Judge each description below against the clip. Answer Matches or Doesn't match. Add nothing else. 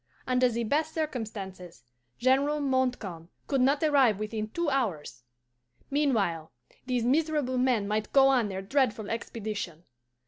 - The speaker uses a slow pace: Matches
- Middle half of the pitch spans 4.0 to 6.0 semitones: Matches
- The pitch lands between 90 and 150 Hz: Doesn't match